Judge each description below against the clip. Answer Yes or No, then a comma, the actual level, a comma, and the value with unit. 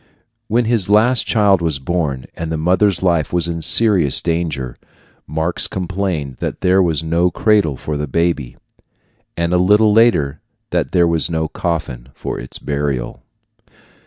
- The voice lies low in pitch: Yes, very low, 85 Hz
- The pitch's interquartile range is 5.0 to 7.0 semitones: No, average, 4.0 semitones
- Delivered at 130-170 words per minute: Yes, average, 155 wpm